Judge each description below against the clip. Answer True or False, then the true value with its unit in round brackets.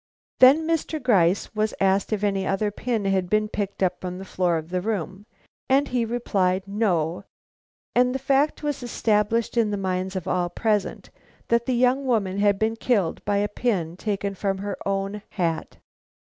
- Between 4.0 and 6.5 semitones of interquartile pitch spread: False (3.6 semitones)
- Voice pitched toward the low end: False (205 Hz)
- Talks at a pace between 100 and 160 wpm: False (180 wpm)